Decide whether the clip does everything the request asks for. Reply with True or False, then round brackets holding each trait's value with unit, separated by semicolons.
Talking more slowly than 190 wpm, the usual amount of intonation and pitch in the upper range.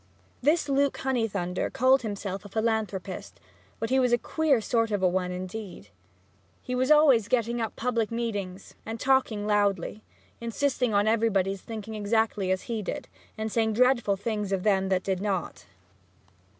True (160 wpm; 3.4 semitones; 220 Hz)